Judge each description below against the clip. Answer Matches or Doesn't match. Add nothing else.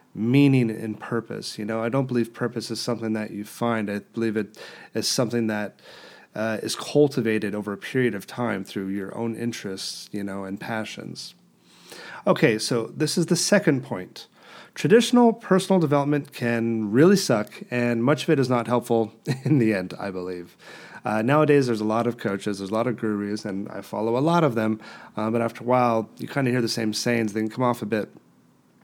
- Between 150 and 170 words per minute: Doesn't match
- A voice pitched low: Matches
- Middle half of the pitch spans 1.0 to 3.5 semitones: Matches